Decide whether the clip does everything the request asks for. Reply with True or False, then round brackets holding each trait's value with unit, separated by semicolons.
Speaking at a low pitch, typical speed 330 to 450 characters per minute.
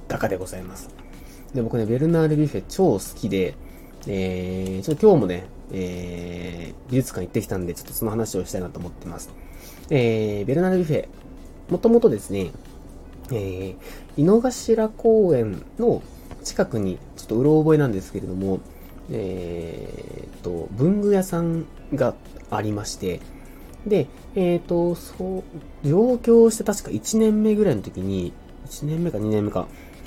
False (105 Hz; 295 characters per minute)